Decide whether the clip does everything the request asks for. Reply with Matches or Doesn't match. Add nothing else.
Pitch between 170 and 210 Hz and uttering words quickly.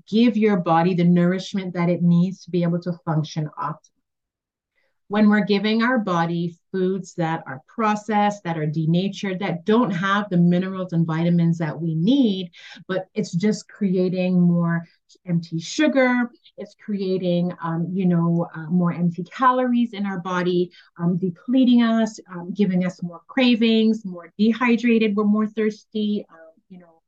Doesn't match